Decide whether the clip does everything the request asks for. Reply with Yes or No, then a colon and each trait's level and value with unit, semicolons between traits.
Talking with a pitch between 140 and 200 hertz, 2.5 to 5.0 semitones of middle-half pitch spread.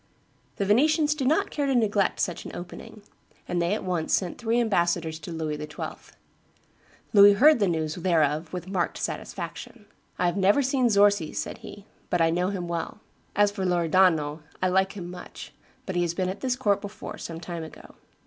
Yes: medium, 185 Hz; average, 3.4 semitones